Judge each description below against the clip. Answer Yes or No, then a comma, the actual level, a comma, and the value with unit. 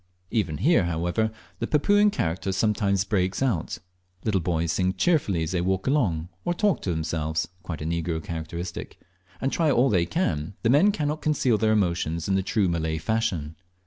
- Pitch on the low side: Yes, very low, 95 Hz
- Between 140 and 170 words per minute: No, average, 180 wpm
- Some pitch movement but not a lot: No, wide, 5.9 semitones